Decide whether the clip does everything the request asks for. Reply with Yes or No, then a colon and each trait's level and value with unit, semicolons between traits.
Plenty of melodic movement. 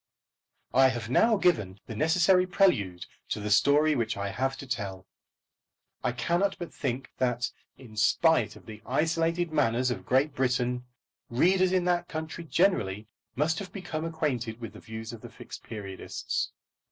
Yes: wide, 6.8 semitones